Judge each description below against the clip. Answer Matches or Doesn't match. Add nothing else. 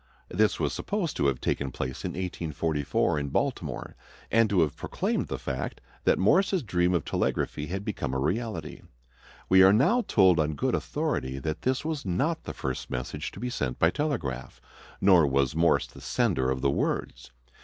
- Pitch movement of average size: Doesn't match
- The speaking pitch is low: Matches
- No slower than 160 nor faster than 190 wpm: Matches